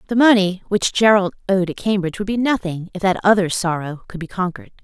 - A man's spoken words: No, female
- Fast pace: Yes, fast, 210 wpm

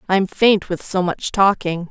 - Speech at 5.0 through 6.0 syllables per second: No, 4.1 syllables/s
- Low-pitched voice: No, medium, 185 Hz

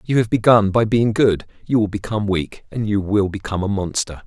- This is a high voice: No, low, 105 Hz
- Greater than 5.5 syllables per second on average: Yes, 5.7 syllables/s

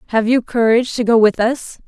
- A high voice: Yes, high, 230 Hz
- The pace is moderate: No, fast, 225 wpm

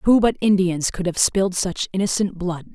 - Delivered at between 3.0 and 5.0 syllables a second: Yes, 4.9 syllables/s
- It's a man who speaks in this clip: No, female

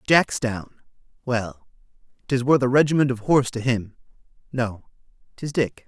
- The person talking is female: No, male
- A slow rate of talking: Yes, slow, 110 wpm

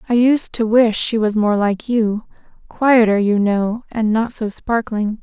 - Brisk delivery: No, average, 170 wpm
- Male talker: No, female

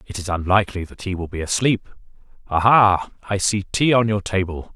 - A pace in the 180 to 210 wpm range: Yes, average, 200 wpm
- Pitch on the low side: Yes, low, 100 Hz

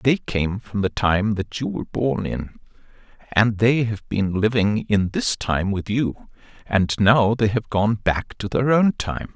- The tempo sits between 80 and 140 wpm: No, average, 190 wpm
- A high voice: No, low, 110 Hz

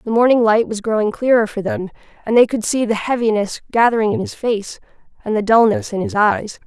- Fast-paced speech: Yes, fast, 215 wpm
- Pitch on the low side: No, high, 220 Hz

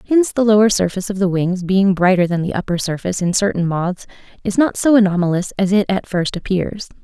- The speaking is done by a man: No, female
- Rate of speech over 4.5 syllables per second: Yes, 6.1 syllables/s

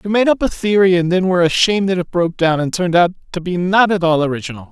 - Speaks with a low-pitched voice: No, medium, 180 Hz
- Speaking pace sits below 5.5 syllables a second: No, 7.1 syllables/s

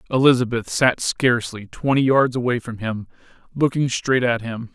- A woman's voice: No, male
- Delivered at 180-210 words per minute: No, average, 150 wpm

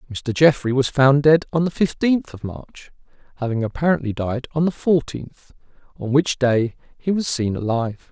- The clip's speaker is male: Yes, male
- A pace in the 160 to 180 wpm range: Yes, average, 170 wpm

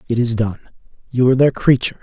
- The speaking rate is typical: Yes, average, 180 wpm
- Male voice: Yes, male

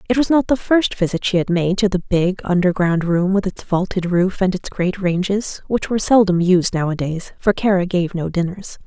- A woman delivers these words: Yes, female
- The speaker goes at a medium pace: No, fast, 210 wpm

